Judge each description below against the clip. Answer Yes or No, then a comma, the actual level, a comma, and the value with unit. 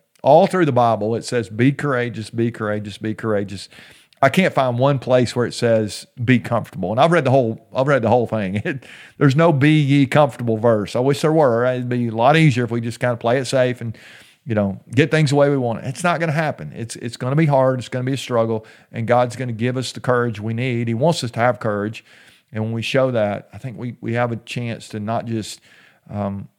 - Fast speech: Yes, fast, 260 wpm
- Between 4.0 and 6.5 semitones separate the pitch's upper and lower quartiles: No, average, 3.2 semitones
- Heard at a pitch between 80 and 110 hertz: No, low, 120 Hz